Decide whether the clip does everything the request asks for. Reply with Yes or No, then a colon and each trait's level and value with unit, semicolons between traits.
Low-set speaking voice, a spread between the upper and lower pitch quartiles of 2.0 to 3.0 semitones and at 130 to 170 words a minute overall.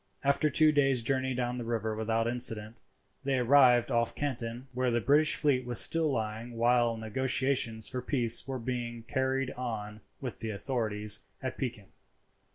Yes: low, 120 Hz; narrow, 2.6 semitones; average, 160 wpm